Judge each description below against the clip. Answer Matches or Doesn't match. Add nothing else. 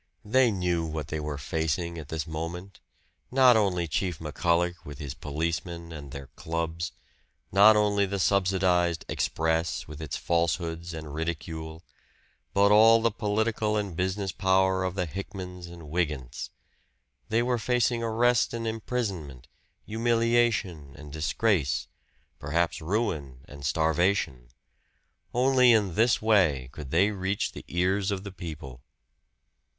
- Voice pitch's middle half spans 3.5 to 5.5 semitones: Matches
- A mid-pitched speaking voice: Doesn't match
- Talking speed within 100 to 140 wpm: Matches